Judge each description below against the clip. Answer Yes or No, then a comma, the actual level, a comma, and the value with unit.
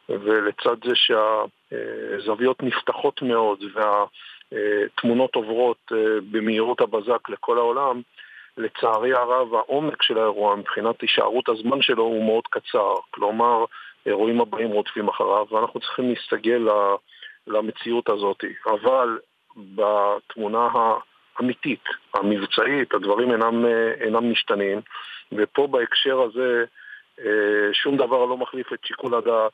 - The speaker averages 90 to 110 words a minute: Yes, average, 105 wpm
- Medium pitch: No, low, 125 Hz